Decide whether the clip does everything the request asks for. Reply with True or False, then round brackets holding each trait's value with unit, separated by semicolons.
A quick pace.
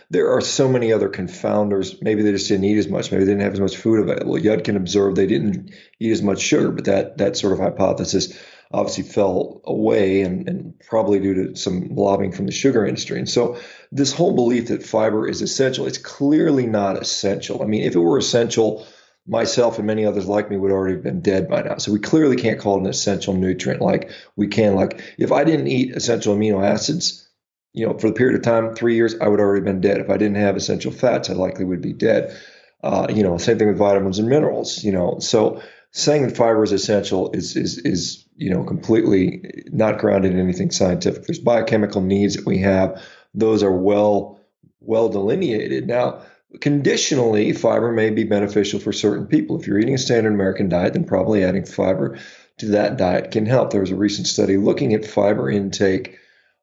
True (210 wpm)